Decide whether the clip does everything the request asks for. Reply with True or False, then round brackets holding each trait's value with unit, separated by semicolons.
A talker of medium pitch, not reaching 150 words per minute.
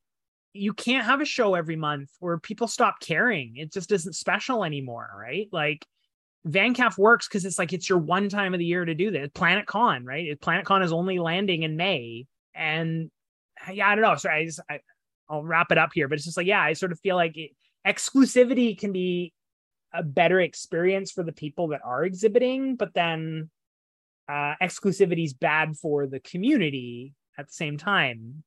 False (175 Hz; 195 wpm)